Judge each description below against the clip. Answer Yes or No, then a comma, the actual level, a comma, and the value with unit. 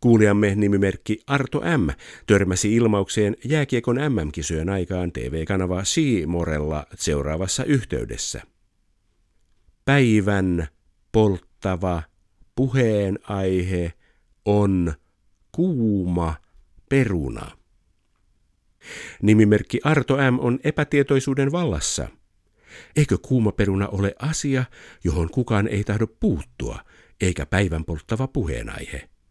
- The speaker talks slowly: Yes, slow, 80 wpm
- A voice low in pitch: Yes, low, 100 Hz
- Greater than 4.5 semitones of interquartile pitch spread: Yes, average, 5.2 semitones